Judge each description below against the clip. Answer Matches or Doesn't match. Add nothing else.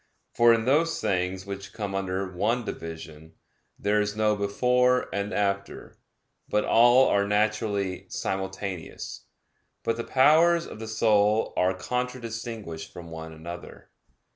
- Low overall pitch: Matches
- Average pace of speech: Doesn't match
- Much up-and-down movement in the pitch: Doesn't match